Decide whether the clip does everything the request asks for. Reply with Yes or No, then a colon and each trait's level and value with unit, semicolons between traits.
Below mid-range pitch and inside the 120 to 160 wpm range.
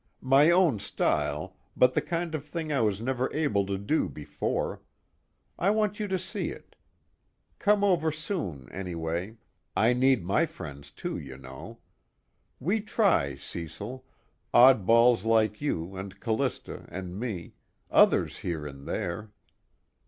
Yes: low, 115 Hz; slow, 135 wpm